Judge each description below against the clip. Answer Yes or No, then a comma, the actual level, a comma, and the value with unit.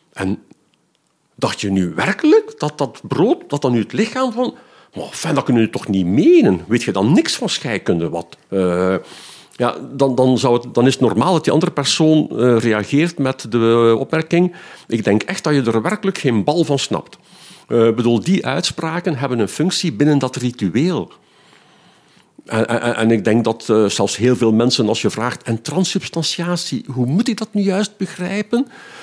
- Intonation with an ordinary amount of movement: No, wide, 7.5 semitones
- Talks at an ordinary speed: Yes, average, 190 wpm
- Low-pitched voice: Yes, low, 130 Hz